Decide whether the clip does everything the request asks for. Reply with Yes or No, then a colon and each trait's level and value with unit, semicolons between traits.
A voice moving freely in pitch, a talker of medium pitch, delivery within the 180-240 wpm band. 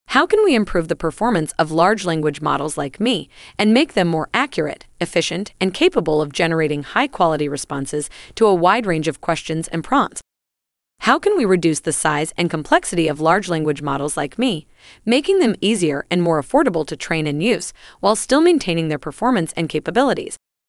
Yes: wide, 5.8 semitones; medium, 165 Hz; average, 185 wpm